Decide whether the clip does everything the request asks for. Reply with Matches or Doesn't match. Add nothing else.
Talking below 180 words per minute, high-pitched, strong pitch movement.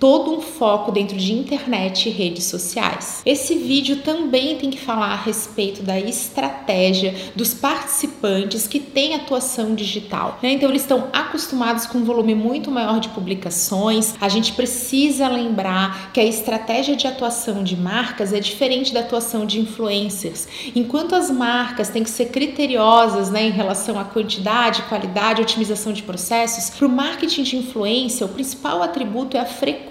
Doesn't match